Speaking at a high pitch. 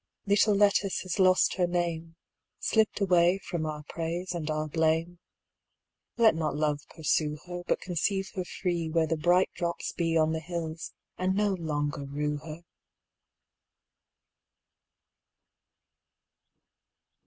No: medium, 170 Hz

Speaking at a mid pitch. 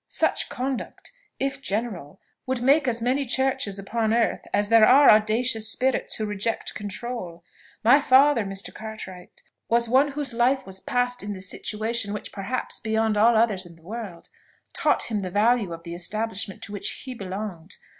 No: high, 220 Hz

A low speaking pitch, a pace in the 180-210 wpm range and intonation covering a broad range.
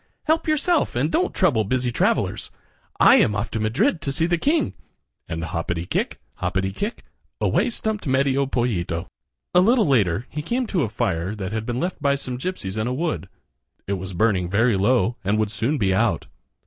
Yes: low, 120 Hz; average, 190 wpm; wide, 8.9 semitones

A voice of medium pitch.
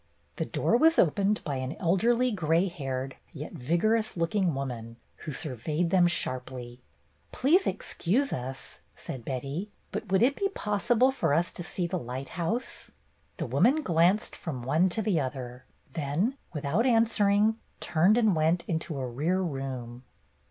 Yes: medium, 170 Hz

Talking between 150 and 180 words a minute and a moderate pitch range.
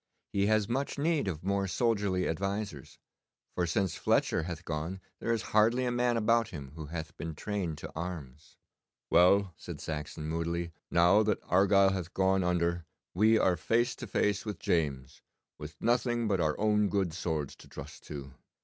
Yes: average, 170 wpm; average, 4.6 semitones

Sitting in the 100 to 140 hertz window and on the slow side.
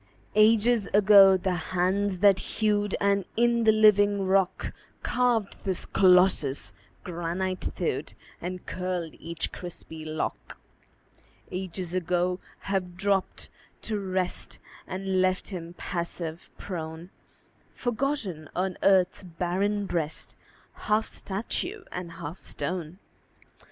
No: medium, 185 Hz; slow, 105 wpm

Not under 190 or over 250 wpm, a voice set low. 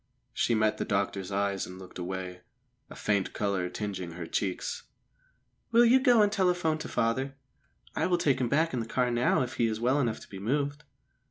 Yes: average, 200 wpm; low, 115 Hz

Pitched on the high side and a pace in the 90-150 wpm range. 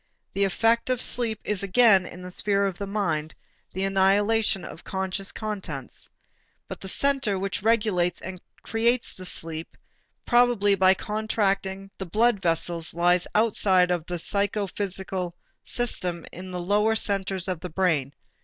Yes: high, 195 Hz; average, 145 wpm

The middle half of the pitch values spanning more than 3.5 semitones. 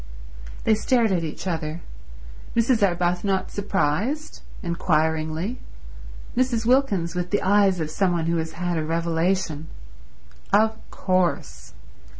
Yes: average, 4.0 semitones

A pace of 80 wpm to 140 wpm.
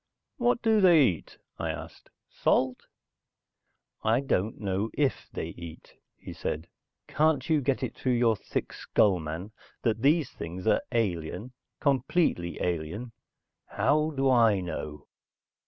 Yes: slow, 135 wpm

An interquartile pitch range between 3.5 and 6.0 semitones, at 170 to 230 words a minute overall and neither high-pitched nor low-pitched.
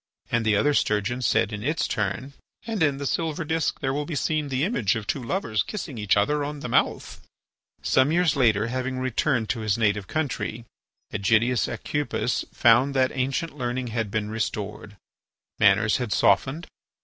No: average, 5.2 semitones; average, 175 wpm; low, 125 Hz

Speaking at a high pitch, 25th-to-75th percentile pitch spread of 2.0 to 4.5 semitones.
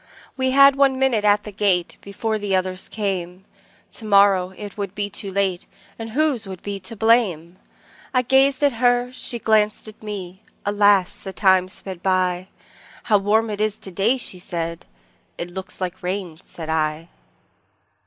Yes: high, 200 Hz; average, 3.3 semitones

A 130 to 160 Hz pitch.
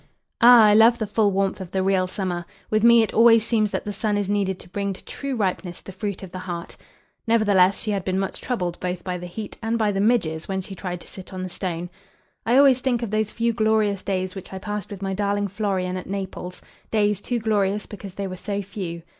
No: high, 200 Hz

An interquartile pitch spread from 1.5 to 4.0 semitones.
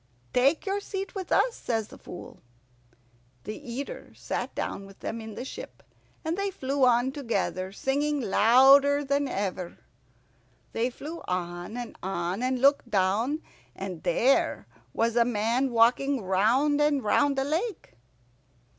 No: average, 5.3 semitones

